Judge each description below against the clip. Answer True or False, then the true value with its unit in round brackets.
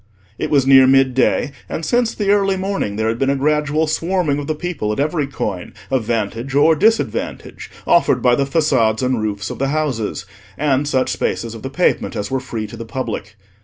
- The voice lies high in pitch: False (135 Hz)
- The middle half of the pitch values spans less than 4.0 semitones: False (5.1 semitones)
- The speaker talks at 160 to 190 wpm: False (205 wpm)